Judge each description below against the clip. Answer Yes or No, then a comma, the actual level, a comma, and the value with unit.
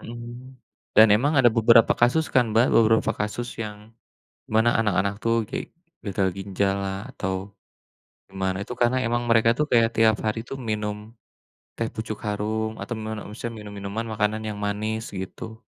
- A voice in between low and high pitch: No, low, 110 Hz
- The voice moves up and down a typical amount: No, narrow, 2.1 semitones